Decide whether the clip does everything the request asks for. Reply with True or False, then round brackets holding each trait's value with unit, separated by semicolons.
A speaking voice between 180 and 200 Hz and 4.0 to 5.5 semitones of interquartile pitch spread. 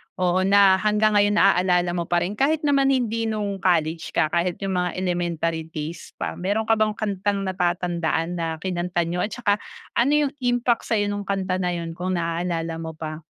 False (185 Hz; 3.3 semitones)